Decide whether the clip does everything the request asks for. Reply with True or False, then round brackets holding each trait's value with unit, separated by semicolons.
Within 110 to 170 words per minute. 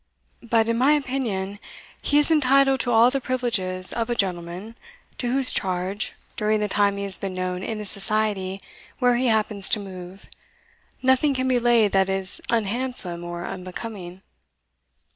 True (160 wpm)